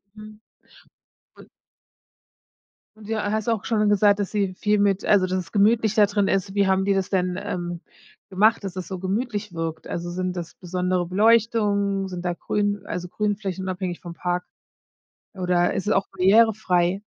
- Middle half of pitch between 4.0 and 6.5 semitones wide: No, narrow, 2.4 semitones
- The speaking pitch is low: No, high, 195 Hz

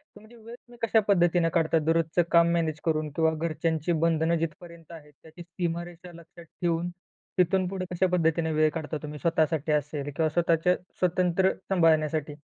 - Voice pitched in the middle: Yes, medium, 165 Hz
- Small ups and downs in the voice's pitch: Yes, narrow, 1.8 semitones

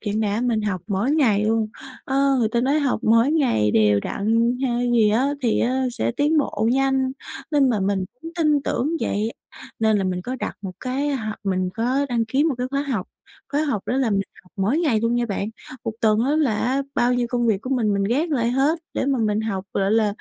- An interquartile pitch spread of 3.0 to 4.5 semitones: Yes, average, 4.2 semitones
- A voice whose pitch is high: Yes, high, 235 Hz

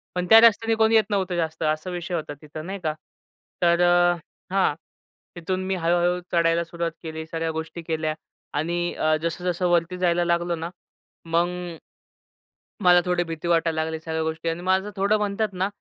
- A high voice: No, medium, 175 Hz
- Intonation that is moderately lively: No, narrow, 2.0 semitones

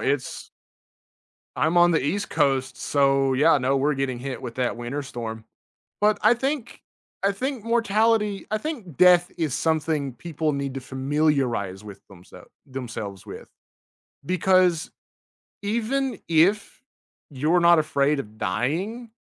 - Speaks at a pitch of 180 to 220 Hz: No, medium, 150 Hz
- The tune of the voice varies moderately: No, wide, 6.8 semitones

